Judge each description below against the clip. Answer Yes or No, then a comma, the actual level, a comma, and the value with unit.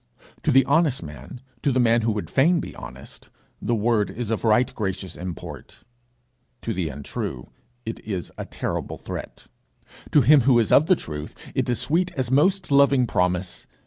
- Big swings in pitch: Yes, wide, 6.7 semitones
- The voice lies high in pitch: No, low, 120 Hz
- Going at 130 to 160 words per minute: No, average, 175 wpm